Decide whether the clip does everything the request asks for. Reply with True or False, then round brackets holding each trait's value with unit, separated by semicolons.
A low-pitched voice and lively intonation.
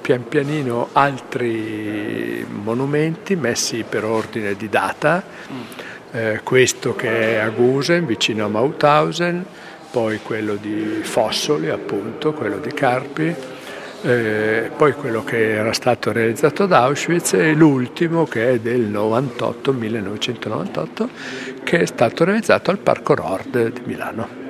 True (120 Hz; 5.7 semitones)